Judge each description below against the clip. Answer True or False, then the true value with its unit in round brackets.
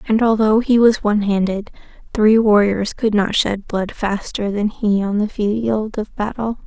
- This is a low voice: False (210 Hz)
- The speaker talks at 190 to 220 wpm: False (180 wpm)